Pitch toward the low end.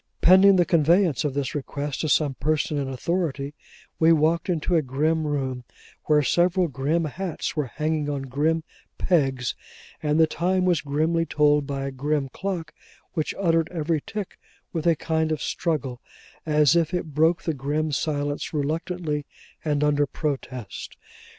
No: medium, 155 Hz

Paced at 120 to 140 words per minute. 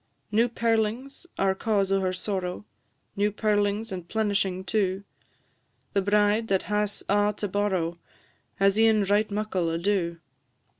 Yes: slow, 135 wpm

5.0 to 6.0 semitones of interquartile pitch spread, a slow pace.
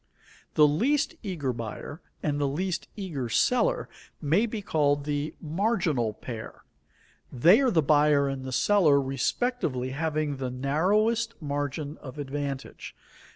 Yes: wide, 5.5 semitones; slow, 130 wpm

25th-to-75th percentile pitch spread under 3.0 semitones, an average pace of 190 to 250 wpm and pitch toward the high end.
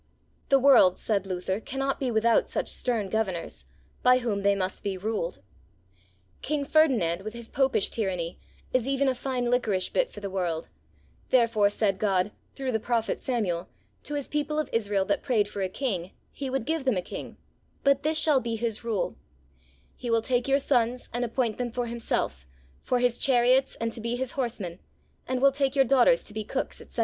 No: average, 4.6 semitones; average, 195 wpm; high, 235 Hz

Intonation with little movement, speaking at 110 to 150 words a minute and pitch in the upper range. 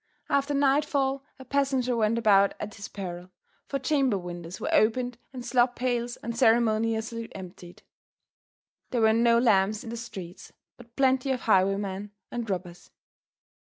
No: average, 4.2 semitones; average, 140 wpm; high, 230 Hz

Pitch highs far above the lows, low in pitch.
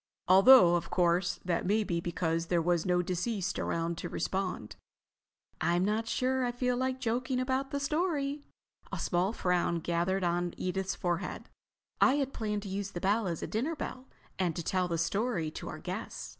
No: wide, 6.2 semitones; high, 190 Hz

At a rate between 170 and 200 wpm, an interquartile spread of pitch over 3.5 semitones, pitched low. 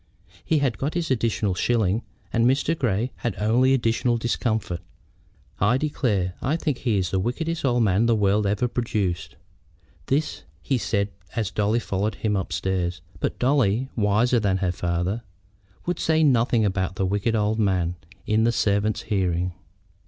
No: average, 160 wpm; average, 4.1 semitones; low, 110 Hz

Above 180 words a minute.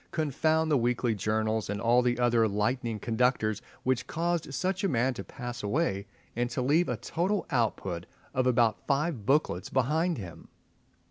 No: average, 160 wpm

